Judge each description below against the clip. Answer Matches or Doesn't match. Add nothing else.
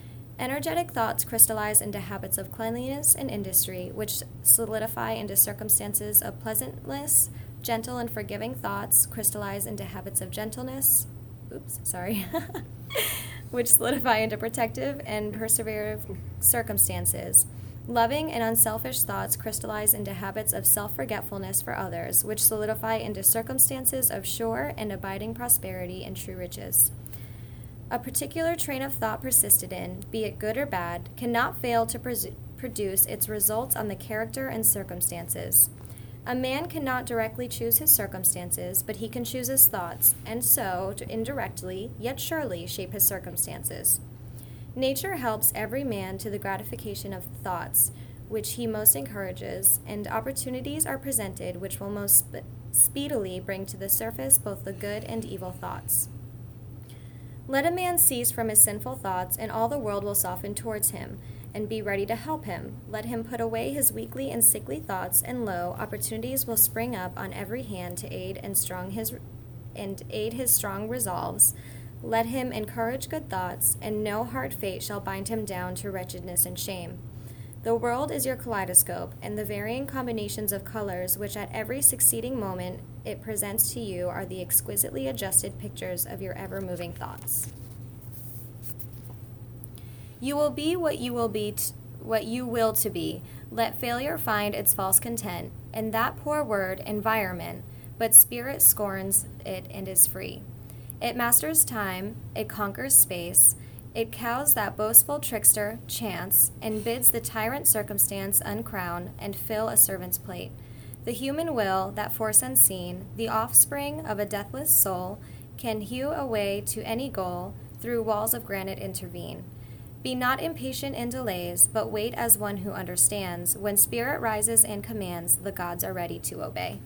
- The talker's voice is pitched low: Matches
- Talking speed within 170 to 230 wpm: Doesn't match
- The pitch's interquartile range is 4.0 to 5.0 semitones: Matches